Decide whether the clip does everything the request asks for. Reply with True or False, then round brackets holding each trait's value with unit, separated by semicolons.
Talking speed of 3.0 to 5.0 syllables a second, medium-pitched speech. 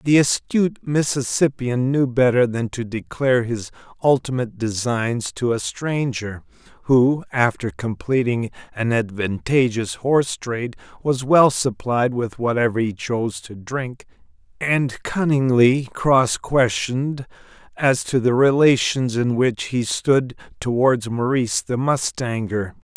False (4.1 syllables/s; 125 Hz)